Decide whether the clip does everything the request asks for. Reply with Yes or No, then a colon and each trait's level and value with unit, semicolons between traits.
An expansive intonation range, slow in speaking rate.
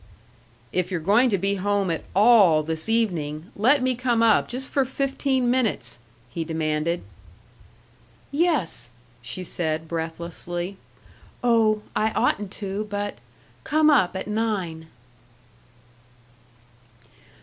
Yes: wide, 6.2 semitones; slow, 115 wpm